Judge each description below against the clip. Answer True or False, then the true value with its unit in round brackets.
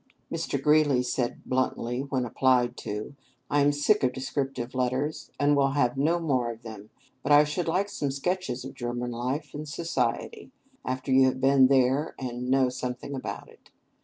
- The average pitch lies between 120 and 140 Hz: True (135 Hz)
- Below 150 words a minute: False (175 wpm)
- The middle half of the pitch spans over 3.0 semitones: False (2.6 semitones)